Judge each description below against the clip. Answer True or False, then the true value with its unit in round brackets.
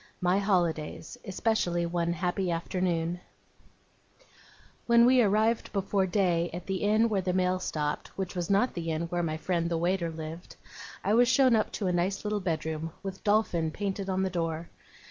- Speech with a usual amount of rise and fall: True (3.1 semitones)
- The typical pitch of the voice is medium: True (180 Hz)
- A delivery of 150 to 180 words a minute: True (175 wpm)